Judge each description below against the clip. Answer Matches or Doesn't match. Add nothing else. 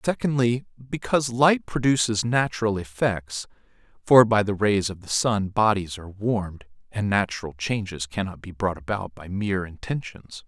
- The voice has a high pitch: Doesn't match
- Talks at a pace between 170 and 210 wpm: Doesn't match